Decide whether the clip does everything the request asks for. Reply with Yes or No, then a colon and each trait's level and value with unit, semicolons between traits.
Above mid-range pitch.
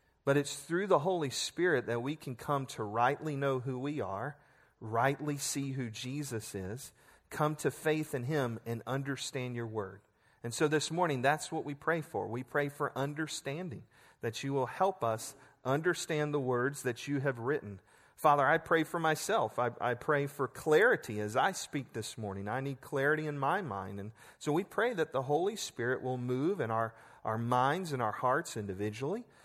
No: low, 135 Hz